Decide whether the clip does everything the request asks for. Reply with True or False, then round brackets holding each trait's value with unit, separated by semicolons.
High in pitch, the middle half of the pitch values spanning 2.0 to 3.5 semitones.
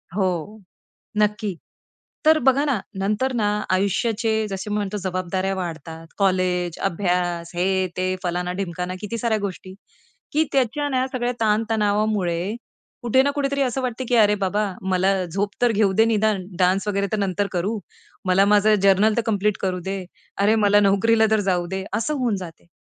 True (200 Hz; 3.2 semitones)